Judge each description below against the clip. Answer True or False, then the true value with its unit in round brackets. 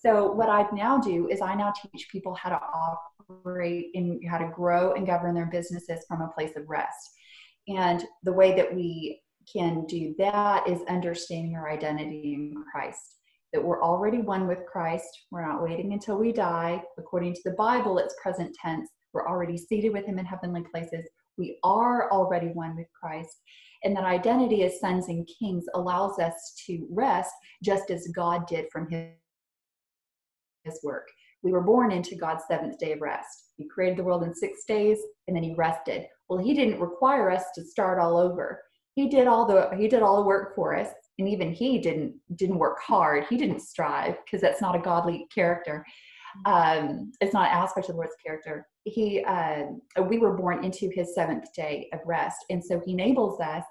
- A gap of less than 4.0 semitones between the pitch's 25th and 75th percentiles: True (3.2 semitones)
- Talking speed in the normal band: True (195 wpm)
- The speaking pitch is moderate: True (180 Hz)